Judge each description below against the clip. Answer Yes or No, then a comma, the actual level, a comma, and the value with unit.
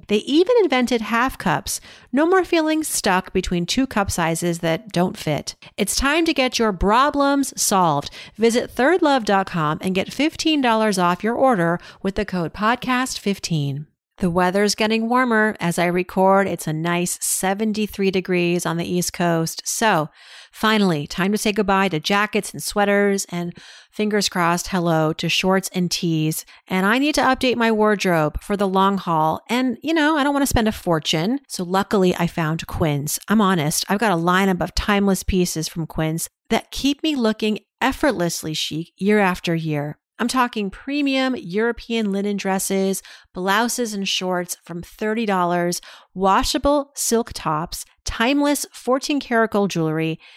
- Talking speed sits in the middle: Yes, average, 160 wpm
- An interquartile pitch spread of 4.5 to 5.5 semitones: Yes, average, 5.0 semitones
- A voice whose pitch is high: Yes, high, 195 Hz